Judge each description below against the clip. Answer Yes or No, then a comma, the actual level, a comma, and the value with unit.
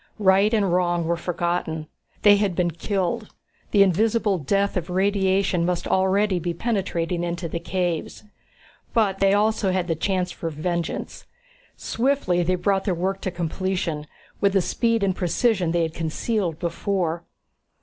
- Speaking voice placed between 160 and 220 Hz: Yes, medium, 185 Hz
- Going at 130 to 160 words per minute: Yes, average, 150 wpm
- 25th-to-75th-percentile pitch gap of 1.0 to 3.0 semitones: Yes, narrow, 2.5 semitones